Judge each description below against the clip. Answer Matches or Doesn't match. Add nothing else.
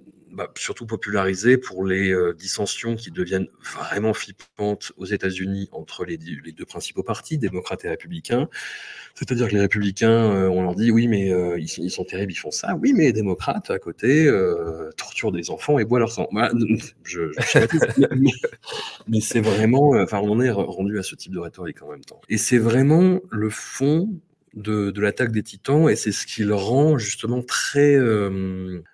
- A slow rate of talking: Doesn't match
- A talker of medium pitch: Doesn't match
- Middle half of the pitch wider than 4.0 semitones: Matches